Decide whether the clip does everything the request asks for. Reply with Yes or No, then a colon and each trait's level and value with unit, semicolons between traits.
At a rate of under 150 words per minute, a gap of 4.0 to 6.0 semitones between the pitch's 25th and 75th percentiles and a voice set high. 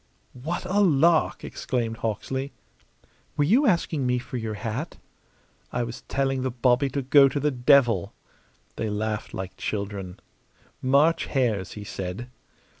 No: average, 140 wpm; average, 4.4 semitones; low, 125 Hz